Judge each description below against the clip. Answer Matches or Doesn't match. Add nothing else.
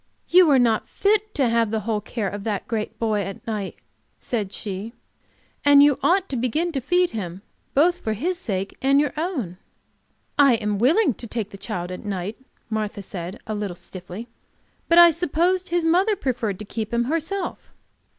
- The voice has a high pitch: Matches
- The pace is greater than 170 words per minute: Matches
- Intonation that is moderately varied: Doesn't match